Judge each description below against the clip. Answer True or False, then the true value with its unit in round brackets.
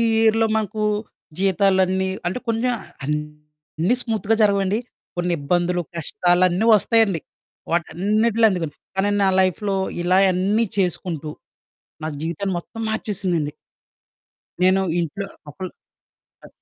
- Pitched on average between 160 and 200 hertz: True (190 Hz)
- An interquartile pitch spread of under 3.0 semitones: False (3.5 semitones)